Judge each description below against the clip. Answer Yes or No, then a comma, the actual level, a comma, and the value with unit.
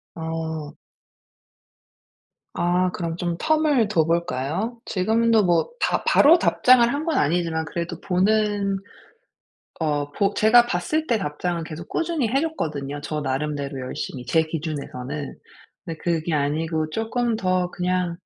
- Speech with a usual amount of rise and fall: No, wide, 5.8 semitones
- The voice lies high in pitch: No, medium, 175 Hz